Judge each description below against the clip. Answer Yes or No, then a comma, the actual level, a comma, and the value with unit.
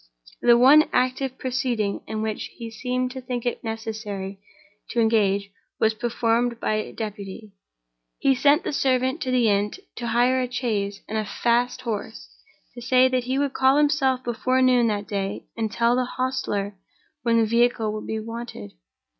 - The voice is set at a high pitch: Yes, high, 235 Hz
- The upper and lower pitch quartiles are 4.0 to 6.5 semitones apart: No, average, 2.8 semitones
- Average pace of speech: Yes, average, 170 wpm